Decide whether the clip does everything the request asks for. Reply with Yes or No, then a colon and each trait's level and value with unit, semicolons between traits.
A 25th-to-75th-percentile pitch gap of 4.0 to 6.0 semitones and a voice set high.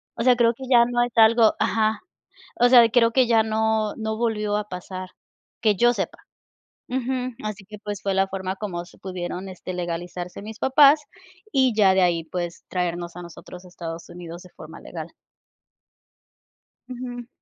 Yes: average, 4.6 semitones; high, 210 Hz